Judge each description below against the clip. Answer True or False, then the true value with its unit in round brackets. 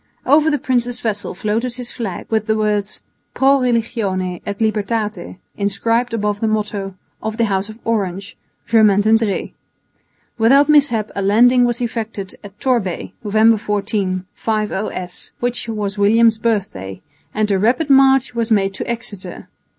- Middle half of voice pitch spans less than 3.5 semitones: True (2.8 semitones)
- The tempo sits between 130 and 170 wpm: True (150 wpm)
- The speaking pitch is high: True (220 Hz)